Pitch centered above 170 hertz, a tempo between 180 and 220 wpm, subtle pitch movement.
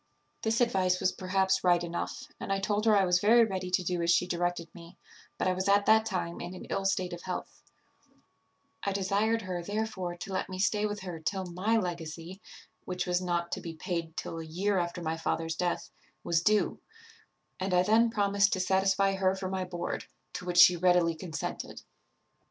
Yes: medium, 185 Hz; average, 200 wpm; narrow, 2.2 semitones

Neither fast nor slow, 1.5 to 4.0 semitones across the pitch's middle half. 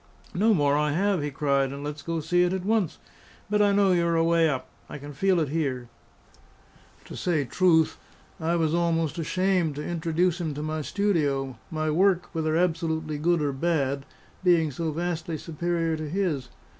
Yes: average, 180 wpm; average, 2.9 semitones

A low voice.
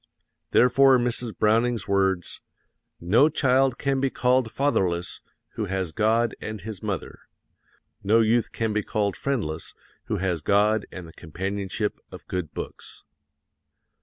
Yes: low, 110 Hz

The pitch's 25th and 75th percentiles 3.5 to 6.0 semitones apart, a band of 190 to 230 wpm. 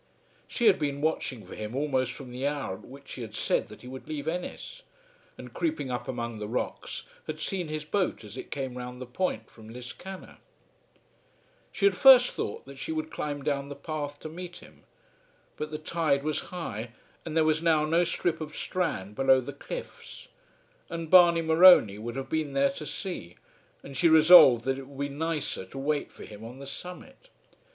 Yes: average, 4.4 semitones; average, 200 wpm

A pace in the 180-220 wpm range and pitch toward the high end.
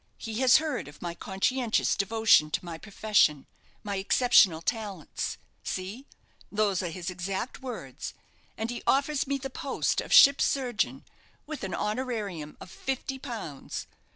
No: average, 145 wpm; high, 215 Hz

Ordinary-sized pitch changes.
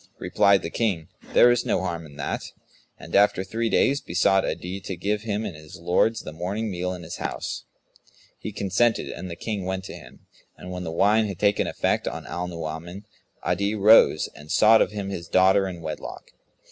Yes: average, 3.3 semitones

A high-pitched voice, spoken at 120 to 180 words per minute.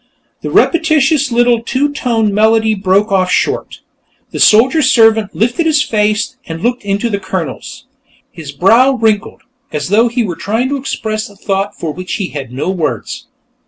Yes: high, 220 Hz; average, 165 wpm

